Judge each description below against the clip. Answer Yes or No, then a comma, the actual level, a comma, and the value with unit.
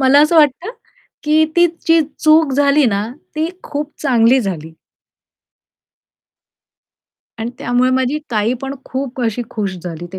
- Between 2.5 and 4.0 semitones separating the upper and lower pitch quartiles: No, average, 5.0 semitones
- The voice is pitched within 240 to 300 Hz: Yes, very high, 260 Hz